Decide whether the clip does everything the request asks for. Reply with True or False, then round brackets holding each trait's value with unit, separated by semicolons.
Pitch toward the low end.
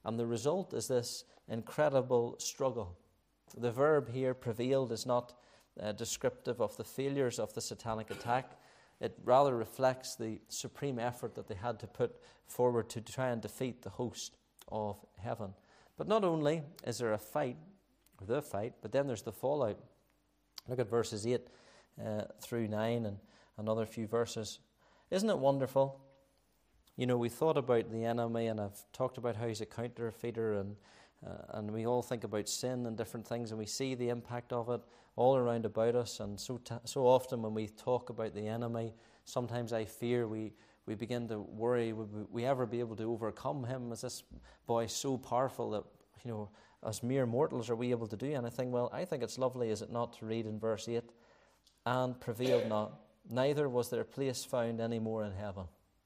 True (120 Hz)